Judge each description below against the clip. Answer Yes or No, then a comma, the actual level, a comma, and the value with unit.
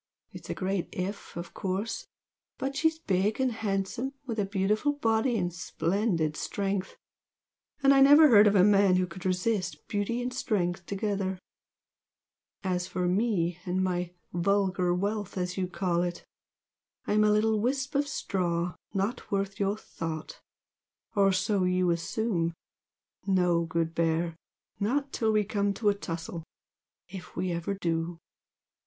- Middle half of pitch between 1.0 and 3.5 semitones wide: Yes, average, 3.2 semitones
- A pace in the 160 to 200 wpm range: No, average, 150 wpm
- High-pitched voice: Yes, high, 195 Hz